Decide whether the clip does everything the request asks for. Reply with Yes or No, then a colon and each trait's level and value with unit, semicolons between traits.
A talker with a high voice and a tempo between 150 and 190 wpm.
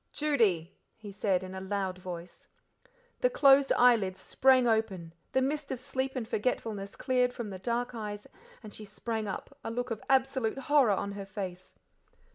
Yes: high, 220 Hz; average, 170 wpm